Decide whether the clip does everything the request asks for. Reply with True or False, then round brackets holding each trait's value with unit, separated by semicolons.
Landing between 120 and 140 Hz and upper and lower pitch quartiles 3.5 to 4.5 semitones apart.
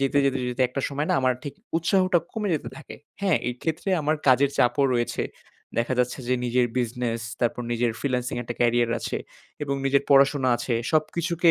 True (135 Hz; 3.9 semitones)